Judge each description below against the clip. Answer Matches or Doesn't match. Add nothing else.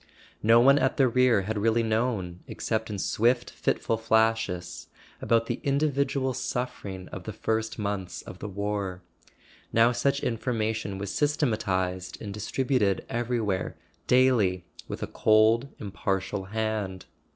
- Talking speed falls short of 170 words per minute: Matches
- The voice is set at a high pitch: Doesn't match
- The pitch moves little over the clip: Doesn't match